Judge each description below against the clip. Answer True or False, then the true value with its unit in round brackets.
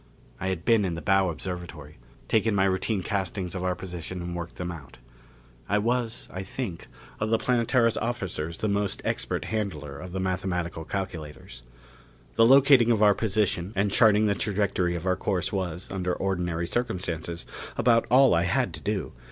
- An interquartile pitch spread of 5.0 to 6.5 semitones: False (3.6 semitones)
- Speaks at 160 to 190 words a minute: True (175 wpm)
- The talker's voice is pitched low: True (95 Hz)